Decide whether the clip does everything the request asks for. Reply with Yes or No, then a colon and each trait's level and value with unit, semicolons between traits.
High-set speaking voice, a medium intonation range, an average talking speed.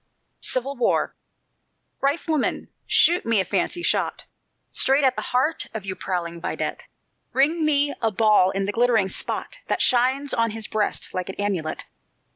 No: high, 230 Hz; wide, 6.1 semitones; average, 155 wpm